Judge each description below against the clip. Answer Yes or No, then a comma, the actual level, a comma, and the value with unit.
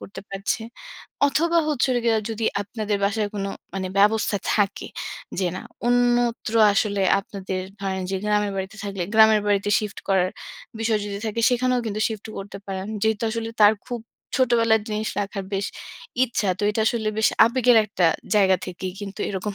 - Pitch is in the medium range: No, high, 210 Hz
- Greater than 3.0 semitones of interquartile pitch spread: No, narrow, 2.4 semitones